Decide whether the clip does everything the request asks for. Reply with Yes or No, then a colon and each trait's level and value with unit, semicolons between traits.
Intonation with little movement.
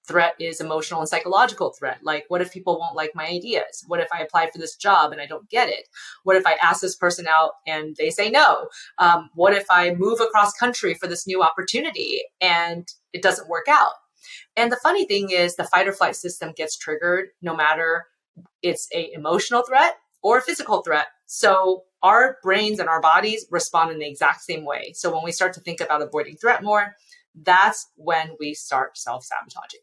No: average, 3.9 semitones